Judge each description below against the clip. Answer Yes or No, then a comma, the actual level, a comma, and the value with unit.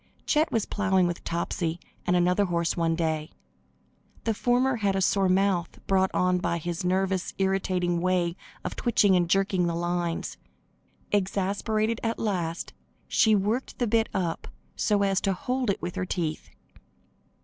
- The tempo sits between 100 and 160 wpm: Yes, average, 155 wpm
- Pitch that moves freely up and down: No, average, 2.9 semitones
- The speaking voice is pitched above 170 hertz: Yes, medium, 185 Hz